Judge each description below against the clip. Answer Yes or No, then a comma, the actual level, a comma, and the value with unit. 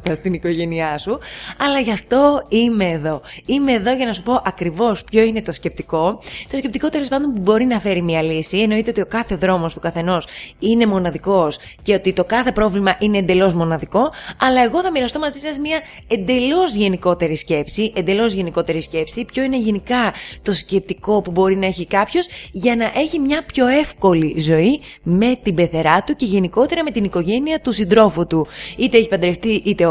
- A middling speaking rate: No, fast, 185 wpm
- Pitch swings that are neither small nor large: No, wide, 5.9 semitones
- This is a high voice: Yes, high, 205 Hz